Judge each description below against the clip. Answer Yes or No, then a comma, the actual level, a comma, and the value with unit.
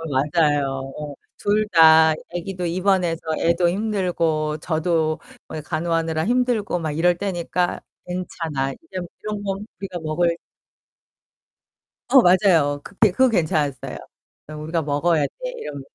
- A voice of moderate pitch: Yes, medium, 170 Hz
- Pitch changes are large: No, average, 3.3 semitones